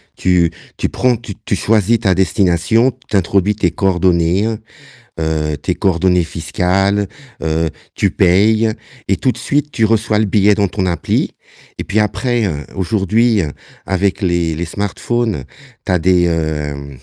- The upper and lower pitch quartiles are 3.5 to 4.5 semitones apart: Yes, average, 4.0 semitones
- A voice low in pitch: Yes, very low, 95 Hz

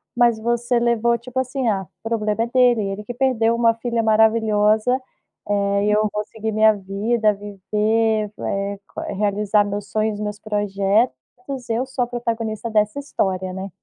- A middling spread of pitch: No, narrow, 2.3 semitones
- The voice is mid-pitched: No, high, 220 Hz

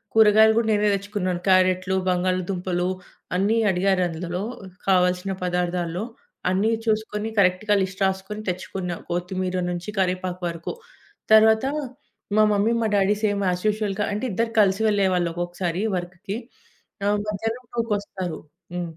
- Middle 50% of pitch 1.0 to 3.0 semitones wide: Yes, narrow, 2.6 semitones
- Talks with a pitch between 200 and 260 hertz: No, high, 190 Hz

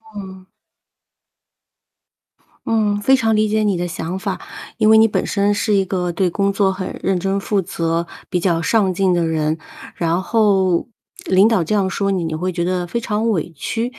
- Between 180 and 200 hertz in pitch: Yes, high, 190 Hz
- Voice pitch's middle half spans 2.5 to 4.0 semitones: Yes, average, 3.1 semitones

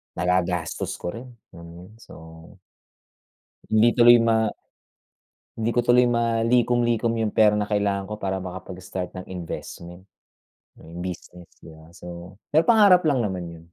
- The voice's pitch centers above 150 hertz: No, low, 105 Hz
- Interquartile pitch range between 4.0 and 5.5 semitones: Yes, average, 4.7 semitones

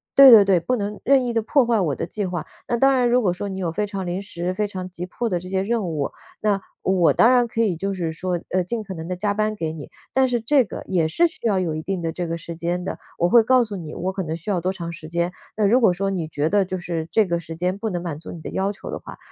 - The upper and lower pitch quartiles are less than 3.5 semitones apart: No, average, 3.9 semitones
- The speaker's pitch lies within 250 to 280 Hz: No, high, 190 Hz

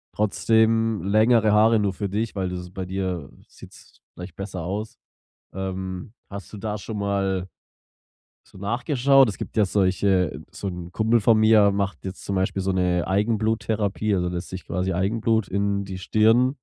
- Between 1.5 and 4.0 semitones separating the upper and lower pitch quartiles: Yes, average, 2.7 semitones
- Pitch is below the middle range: Yes, low, 100 Hz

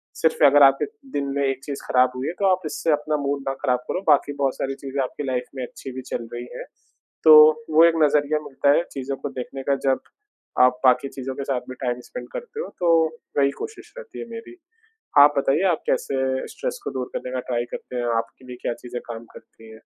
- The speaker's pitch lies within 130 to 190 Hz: Yes, medium, 140 Hz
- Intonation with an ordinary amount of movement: Yes, average, 3.3 semitones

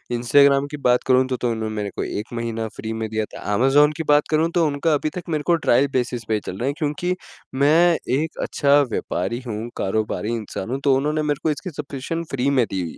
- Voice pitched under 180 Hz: Yes, low, 135 Hz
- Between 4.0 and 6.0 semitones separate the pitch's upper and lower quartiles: Yes, average, 4.7 semitones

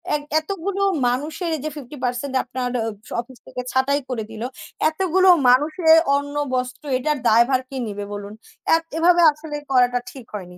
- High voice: Yes, very high, 270 Hz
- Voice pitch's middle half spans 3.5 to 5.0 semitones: Yes, average, 4.0 semitones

